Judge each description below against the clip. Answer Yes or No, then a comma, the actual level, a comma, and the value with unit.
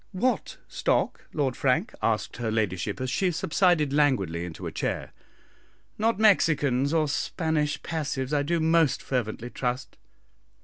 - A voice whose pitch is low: No, medium, 145 Hz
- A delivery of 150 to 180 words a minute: No, slow, 135 wpm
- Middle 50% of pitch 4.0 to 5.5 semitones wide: Yes, average, 4.9 semitones